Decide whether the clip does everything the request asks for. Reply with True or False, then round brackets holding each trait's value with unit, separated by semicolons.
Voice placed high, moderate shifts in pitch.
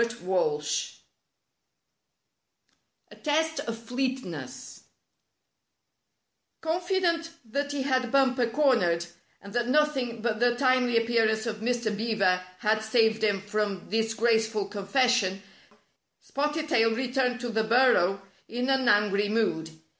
True (230 Hz; 3.6 semitones)